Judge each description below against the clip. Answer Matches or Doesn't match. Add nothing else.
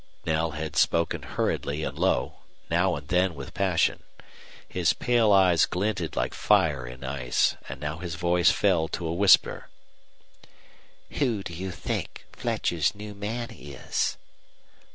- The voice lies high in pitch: Doesn't match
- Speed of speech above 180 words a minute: Doesn't match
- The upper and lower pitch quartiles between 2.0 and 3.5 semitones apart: Doesn't match